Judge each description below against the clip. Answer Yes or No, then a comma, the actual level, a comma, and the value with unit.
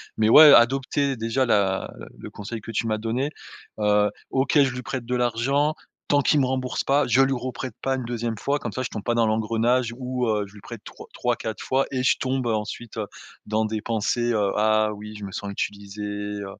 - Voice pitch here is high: No, low, 115 Hz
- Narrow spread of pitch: No, average, 3.3 semitones